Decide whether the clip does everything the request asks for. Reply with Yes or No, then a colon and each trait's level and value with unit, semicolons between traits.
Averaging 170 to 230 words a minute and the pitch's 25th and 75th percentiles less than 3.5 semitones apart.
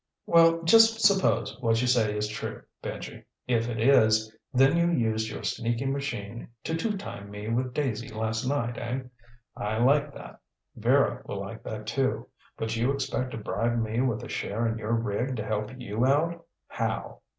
No: average, 180 wpm; average, 3.9 semitones